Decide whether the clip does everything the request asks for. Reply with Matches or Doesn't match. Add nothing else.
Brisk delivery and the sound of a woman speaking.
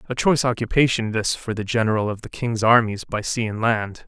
Doesn't match